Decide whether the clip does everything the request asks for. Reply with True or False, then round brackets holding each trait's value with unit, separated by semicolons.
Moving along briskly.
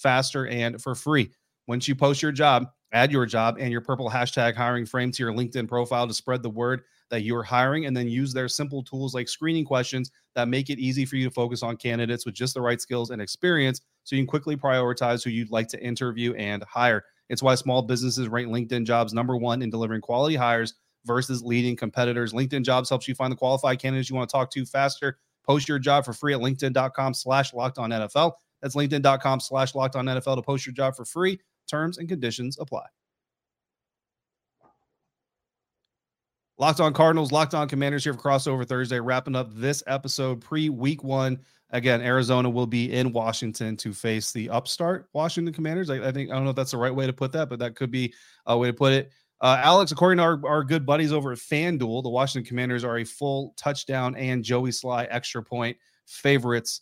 True (210 wpm)